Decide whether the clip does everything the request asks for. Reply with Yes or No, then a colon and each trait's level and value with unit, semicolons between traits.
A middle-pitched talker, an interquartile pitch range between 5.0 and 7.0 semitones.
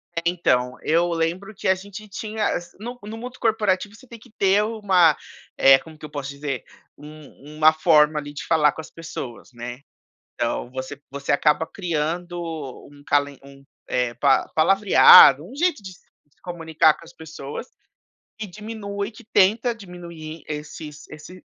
Yes: medium, 165 Hz; average, 5.3 semitones